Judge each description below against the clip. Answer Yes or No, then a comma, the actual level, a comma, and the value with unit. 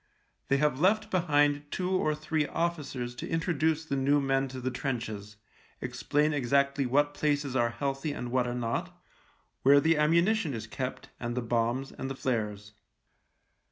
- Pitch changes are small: No, average, 3.5 semitones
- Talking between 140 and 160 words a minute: No, average, 170 wpm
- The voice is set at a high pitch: No, medium, 140 Hz